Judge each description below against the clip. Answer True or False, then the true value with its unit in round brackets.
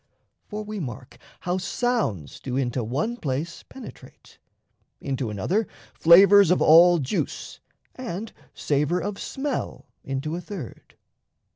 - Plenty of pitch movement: True (7.4 semitones)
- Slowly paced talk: True (120 wpm)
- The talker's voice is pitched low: False (170 Hz)